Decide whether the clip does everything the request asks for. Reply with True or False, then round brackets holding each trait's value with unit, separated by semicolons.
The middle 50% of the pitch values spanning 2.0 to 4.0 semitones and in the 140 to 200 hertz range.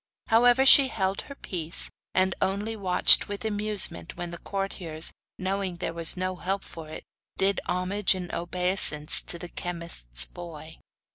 True (2.9 semitones; 185 Hz)